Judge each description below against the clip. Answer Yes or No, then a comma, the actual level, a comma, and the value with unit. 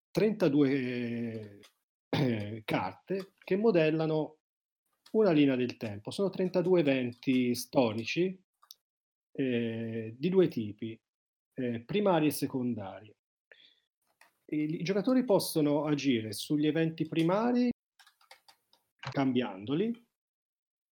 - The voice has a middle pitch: Yes, medium, 150 Hz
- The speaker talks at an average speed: No, slow, 85 wpm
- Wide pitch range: Yes, wide, 7.3 semitones